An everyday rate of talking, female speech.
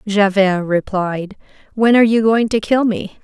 Yes: average, 165 wpm; female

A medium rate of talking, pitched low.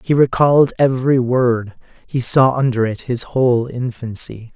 Yes: average, 145 wpm; low, 125 Hz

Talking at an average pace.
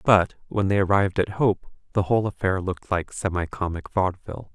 Yes: average, 185 wpm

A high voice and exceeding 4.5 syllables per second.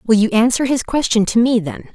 Yes: high, 230 Hz; 6.0 syllables/s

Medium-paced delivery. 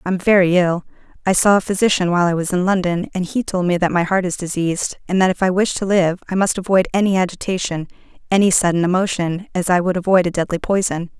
No: fast, 230 wpm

